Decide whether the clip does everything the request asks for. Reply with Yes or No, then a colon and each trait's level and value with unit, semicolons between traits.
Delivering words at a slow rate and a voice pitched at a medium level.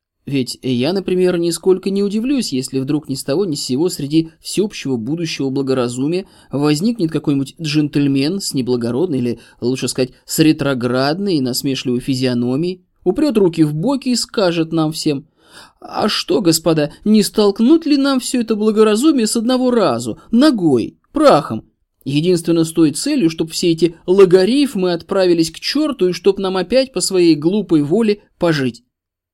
No: average, 150 wpm; medium, 165 Hz